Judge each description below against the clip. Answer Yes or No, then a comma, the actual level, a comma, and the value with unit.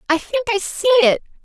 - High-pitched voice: Yes, very high, 385 Hz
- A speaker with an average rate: No, fast, 210 wpm